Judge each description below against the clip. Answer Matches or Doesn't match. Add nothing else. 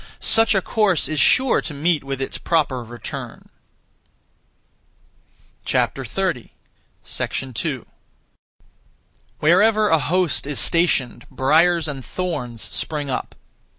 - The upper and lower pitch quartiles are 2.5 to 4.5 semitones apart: Doesn't match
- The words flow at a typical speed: Doesn't match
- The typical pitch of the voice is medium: Matches